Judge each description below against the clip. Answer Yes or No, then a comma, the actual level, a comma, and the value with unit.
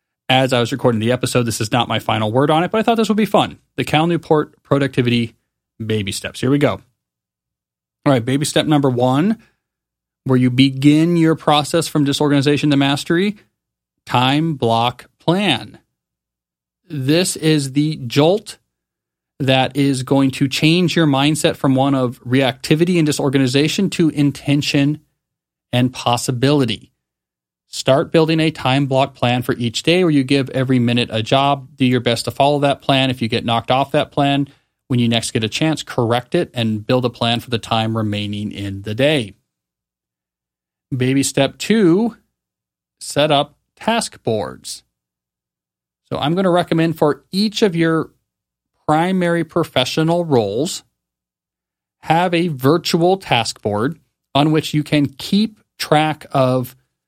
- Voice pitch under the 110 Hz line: No, low, 135 Hz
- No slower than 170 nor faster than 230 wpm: No, average, 155 wpm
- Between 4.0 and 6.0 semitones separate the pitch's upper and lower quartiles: Yes, average, 4.9 semitones